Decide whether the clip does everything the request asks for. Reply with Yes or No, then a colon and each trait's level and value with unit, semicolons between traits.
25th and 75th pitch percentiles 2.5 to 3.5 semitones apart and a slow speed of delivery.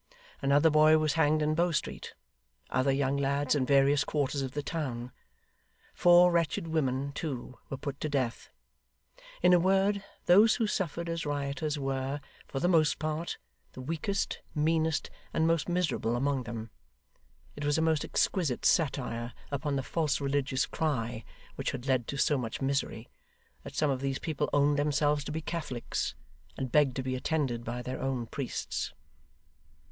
No: average, 3.1 semitones; average, 165 wpm